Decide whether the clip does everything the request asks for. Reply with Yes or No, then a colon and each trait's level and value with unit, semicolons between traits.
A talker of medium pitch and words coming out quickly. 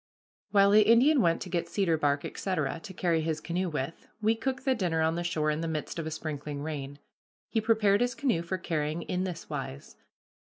Yes: medium, 170 Hz; fast, 210 wpm